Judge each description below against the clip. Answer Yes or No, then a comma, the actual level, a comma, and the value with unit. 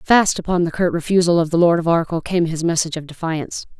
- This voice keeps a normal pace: No, fast, 235 wpm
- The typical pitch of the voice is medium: Yes, medium, 170 Hz